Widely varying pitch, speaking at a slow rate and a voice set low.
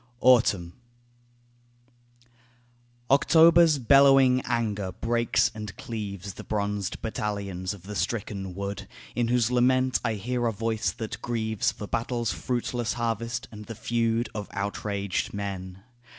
No: average, 3.2 semitones; slow, 120 wpm; low, 110 Hz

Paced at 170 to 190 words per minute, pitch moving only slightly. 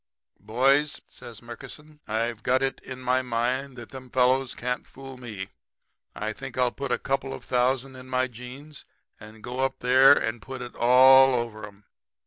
Yes: average, 175 wpm; narrow, 2.0 semitones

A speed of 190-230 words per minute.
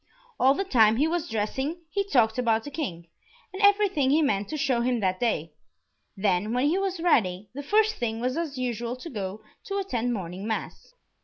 Yes: average, 200 wpm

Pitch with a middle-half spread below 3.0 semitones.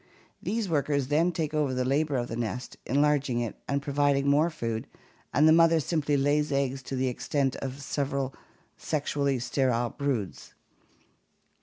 Yes: narrow, 2.5 semitones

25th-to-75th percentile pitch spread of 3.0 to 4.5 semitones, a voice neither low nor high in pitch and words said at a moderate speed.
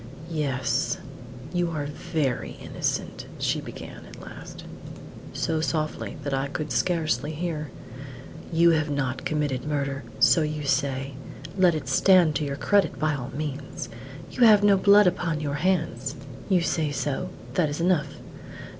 Yes: average, 3.3 semitones; medium, 155 Hz; average, 145 wpm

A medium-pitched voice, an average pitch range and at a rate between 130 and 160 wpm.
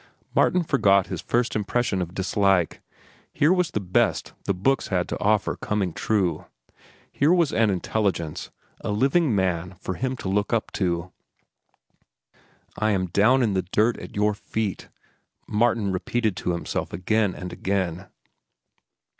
No: low, 100 Hz; average, 3.7 semitones; average, 145 wpm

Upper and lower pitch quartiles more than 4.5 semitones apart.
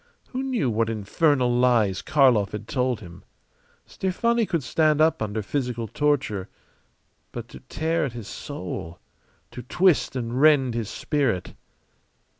Yes: wide, 5.6 semitones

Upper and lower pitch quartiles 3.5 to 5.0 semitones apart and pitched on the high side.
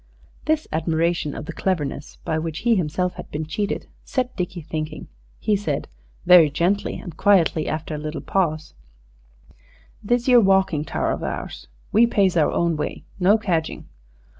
No: average, 4.2 semitones; medium, 170 Hz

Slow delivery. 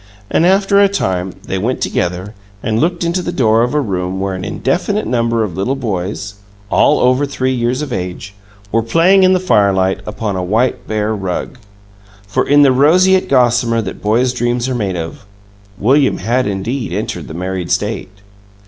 No: average, 180 wpm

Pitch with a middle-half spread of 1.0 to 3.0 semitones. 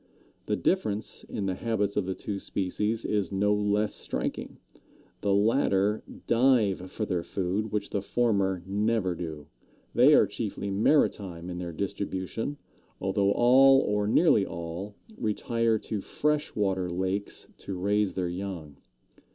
Yes: narrow, 2.6 semitones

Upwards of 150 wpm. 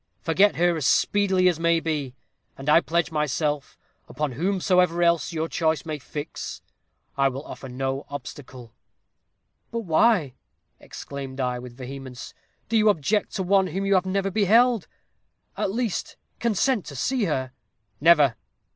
No: average, 145 wpm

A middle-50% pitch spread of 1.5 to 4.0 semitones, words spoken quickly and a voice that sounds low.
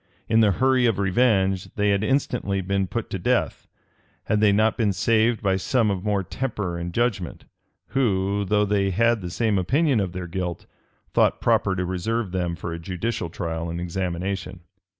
No: average, 3.5 semitones; average, 180 wpm; low, 100 Hz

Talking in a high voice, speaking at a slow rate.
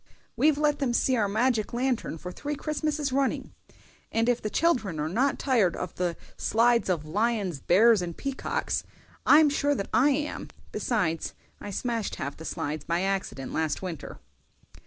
No: high, 225 Hz; average, 165 wpm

